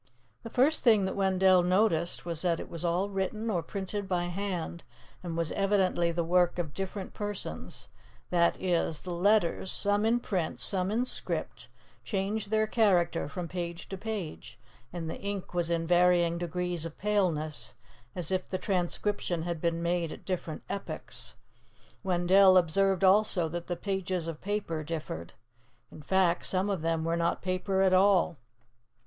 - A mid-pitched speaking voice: Yes, medium, 180 Hz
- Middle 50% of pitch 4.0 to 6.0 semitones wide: No, narrow, 2.6 semitones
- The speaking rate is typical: Yes, average, 165 wpm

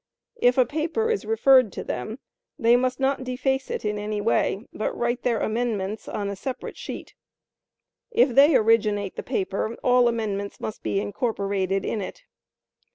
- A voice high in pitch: Yes, high, 230 Hz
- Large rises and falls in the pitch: No, average, 3.8 semitones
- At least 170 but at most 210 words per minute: No, average, 160 wpm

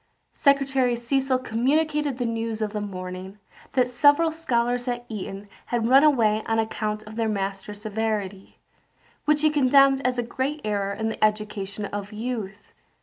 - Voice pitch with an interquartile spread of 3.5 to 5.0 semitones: Yes, average, 3.9 semitones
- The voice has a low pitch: No, high, 230 Hz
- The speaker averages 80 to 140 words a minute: No, average, 155 wpm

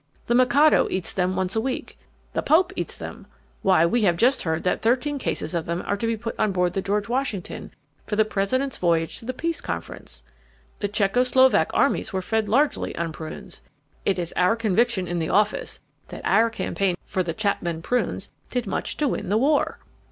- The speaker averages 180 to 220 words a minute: Yes, average, 200 wpm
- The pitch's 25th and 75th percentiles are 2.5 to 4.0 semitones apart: No, average, 5.3 semitones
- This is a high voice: Yes, high, 210 Hz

